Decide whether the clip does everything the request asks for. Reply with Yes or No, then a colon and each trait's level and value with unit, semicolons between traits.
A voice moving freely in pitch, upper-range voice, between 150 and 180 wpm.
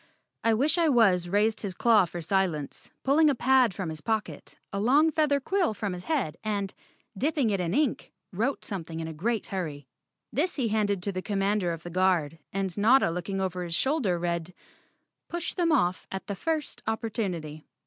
No: wide, 6.4 semitones; high, 200 Hz; average, 190 wpm